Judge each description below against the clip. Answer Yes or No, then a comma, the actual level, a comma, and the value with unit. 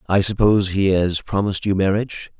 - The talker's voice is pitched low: Yes, very low, 95 Hz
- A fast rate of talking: No, average, 175 wpm